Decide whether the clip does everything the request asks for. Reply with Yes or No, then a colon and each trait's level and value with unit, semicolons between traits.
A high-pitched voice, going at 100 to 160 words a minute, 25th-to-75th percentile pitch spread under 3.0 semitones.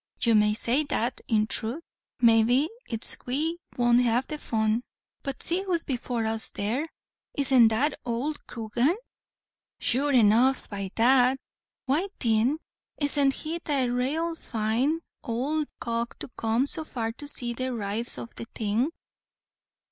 No: high, 245 Hz; average, 145 wpm; average, 4.0 semitones